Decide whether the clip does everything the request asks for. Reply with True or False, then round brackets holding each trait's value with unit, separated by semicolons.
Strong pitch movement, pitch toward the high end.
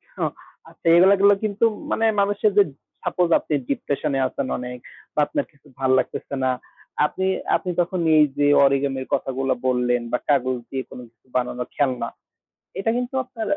False (7.0 semitones; 140 Hz)